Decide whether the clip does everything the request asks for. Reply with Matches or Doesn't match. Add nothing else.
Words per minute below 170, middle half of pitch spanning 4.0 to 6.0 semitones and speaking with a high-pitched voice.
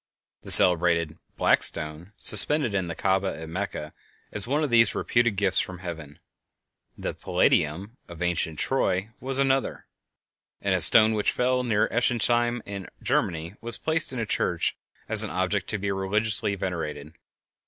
Doesn't match